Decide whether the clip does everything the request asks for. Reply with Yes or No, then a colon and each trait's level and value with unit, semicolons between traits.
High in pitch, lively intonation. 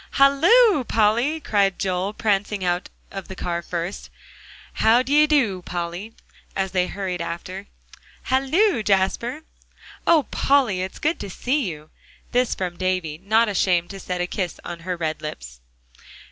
Yes: high, 195 Hz; wide, 5.8 semitones